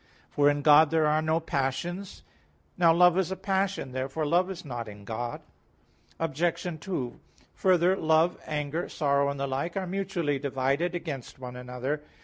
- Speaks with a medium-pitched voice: Yes, medium, 155 Hz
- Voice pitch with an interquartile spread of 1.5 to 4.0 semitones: No, average, 4.4 semitones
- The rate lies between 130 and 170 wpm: Yes, average, 160 wpm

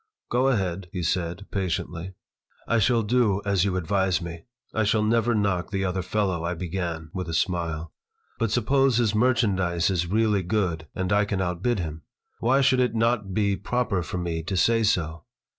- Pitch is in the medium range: No, very low, 95 Hz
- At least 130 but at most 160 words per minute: No, average, 180 wpm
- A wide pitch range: No, average, 4.2 semitones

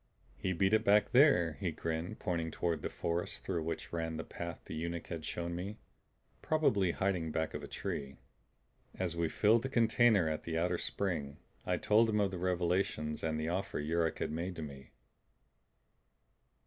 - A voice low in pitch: Yes, very low, 85 Hz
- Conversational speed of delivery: Yes, average, 180 wpm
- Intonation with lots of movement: No, average, 3.4 semitones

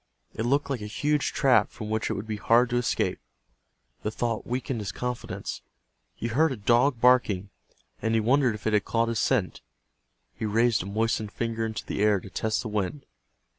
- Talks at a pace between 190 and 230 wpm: Yes, average, 200 wpm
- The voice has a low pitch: Yes, low, 115 Hz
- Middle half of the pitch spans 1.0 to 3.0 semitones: Yes, narrow, 2.6 semitones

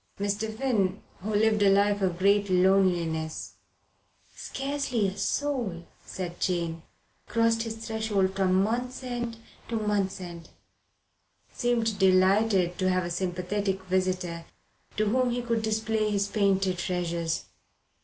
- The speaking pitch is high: Yes, high, 200 Hz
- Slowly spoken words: Yes, slow, 125 wpm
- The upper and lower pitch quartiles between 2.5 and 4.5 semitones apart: Yes, average, 3.2 semitones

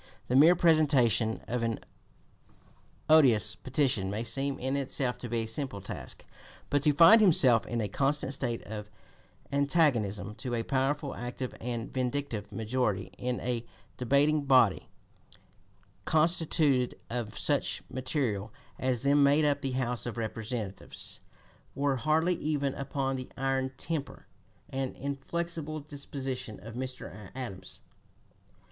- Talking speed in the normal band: No, slow, 130 wpm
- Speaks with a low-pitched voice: Yes, low, 130 Hz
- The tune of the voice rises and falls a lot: No, average, 3.5 semitones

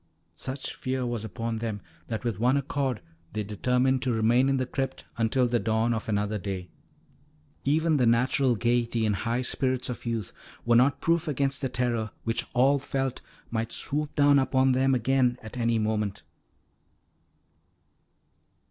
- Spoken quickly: No, average, 155 wpm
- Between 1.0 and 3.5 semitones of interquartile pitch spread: Yes, average, 2.9 semitones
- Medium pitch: No, low, 120 Hz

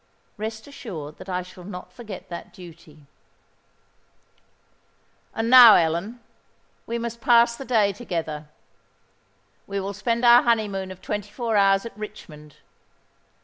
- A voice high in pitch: Yes, high, 205 Hz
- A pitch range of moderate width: Yes, average, 4.4 semitones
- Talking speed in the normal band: No, slow, 130 wpm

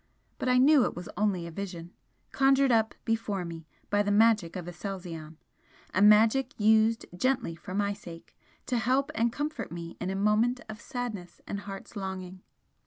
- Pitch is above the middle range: Yes, high, 205 Hz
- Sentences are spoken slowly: No, average, 175 wpm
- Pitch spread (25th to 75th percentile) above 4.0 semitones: Yes, average, 4.6 semitones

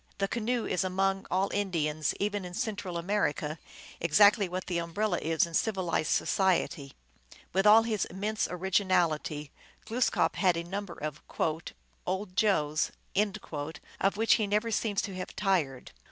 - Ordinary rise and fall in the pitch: Yes, average, 3.6 semitones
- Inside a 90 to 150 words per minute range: Yes, average, 145 wpm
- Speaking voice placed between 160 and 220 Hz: Yes, high, 190 Hz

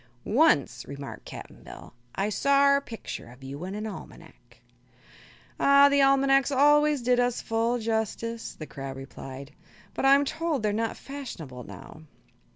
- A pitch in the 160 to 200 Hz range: No, high, 230 Hz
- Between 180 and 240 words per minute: No, average, 150 wpm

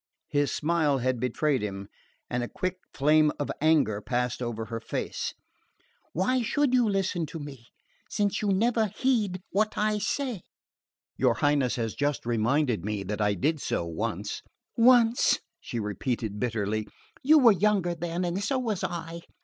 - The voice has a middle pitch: Yes, medium, 155 Hz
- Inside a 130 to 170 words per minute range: Yes, average, 160 wpm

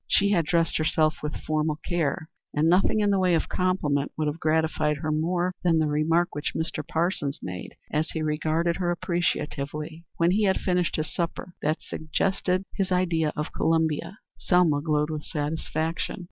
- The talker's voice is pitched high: No, medium, 160 Hz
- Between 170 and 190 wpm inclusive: Yes, average, 175 wpm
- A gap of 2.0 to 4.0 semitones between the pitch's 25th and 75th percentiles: Yes, narrow, 2.5 semitones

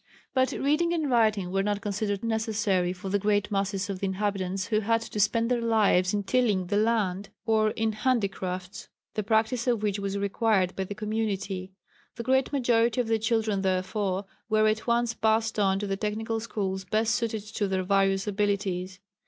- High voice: Yes, high, 210 Hz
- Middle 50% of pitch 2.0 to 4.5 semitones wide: Yes, narrow, 2.5 semitones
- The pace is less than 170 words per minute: No, average, 185 wpm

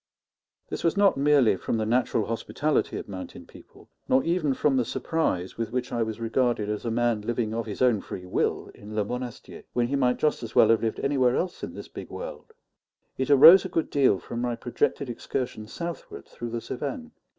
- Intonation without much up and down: No, average, 4.0 semitones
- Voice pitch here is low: Yes, low, 120 Hz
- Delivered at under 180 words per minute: No, fast, 205 wpm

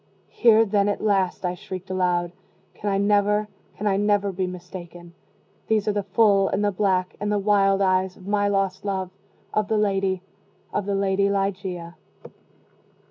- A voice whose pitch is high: Yes, high, 195 Hz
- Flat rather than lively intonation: Yes, narrow, 1.7 semitones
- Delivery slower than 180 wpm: Yes, average, 170 wpm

